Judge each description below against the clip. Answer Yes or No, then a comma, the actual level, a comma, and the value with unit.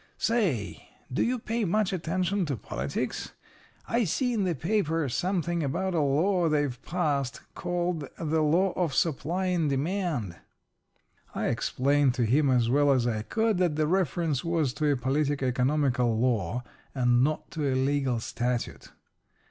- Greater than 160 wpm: No, average, 155 wpm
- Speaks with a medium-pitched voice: Yes, medium, 150 Hz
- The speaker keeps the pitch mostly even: No, wide, 5.5 semitones